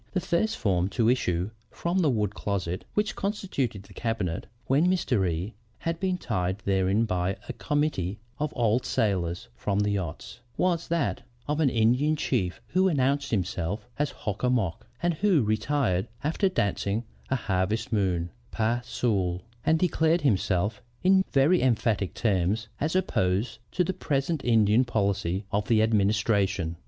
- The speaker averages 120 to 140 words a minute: No, average, 155 wpm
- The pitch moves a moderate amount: No, wide, 7.2 semitones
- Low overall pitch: Yes, low, 110 Hz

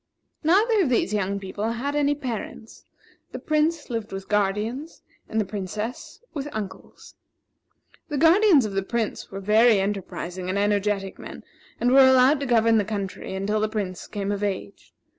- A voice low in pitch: No, high, 215 Hz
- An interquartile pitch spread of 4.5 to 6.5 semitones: Yes, average, 5.1 semitones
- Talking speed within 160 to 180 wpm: Yes, average, 165 wpm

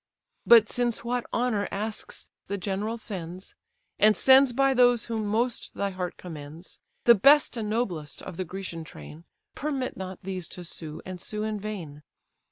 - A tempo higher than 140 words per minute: Yes, average, 165 wpm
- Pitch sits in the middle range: No, high, 205 Hz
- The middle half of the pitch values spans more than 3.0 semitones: Yes, average, 4.8 semitones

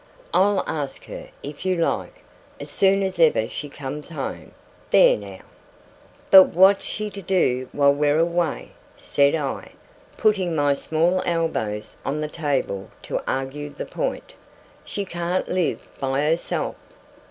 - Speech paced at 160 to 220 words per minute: No, average, 140 wpm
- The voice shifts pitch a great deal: No, average, 4.8 semitones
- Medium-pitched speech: Yes, medium, 160 Hz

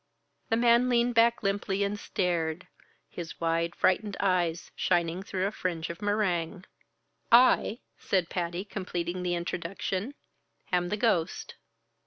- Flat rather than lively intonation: No, average, 3.3 semitones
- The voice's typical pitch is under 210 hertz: Yes, medium, 185 Hz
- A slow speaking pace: Yes, slow, 130 wpm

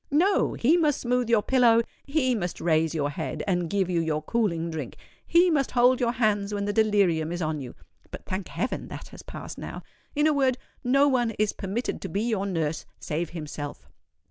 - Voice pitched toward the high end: Yes, high, 205 Hz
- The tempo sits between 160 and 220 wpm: Yes, average, 185 wpm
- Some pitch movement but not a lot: No, wide, 7.0 semitones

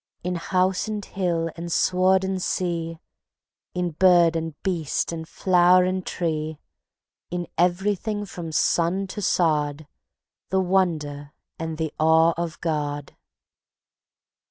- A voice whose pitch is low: No, medium, 175 Hz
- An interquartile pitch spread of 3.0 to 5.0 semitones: No, narrow, 2.4 semitones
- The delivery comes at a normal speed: No, slow, 120 wpm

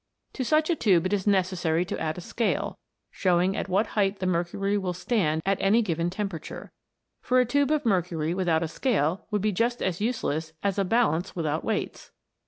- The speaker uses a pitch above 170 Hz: Yes, high, 190 Hz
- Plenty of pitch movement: No, average, 3.8 semitones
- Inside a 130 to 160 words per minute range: No, average, 195 wpm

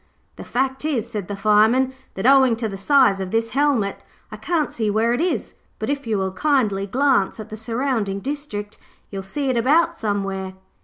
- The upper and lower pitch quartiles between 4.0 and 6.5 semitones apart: Yes, average, 5.1 semitones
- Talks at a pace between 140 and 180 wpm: No, average, 195 wpm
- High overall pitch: Yes, high, 225 Hz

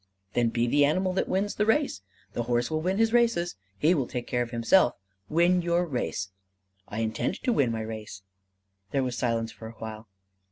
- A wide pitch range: Yes, wide, 7.7 semitones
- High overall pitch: No, low, 125 Hz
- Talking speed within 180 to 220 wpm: Yes, average, 200 wpm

